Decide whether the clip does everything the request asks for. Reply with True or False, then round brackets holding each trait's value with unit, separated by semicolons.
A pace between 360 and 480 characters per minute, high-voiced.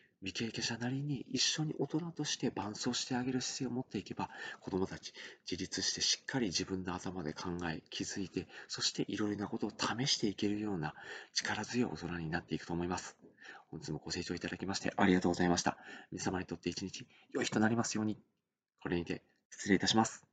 False (430 characters per minute; 100 Hz)